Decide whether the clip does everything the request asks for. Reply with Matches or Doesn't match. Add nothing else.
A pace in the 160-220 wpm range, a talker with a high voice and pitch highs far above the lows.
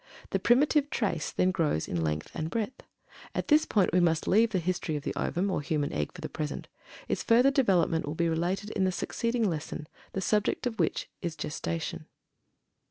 Doesn't match